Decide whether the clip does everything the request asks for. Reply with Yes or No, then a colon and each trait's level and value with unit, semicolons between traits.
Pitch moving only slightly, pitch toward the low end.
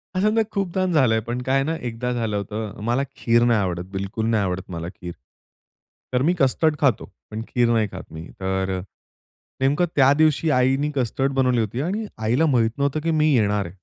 No: average, 5.2 semitones; low, 120 Hz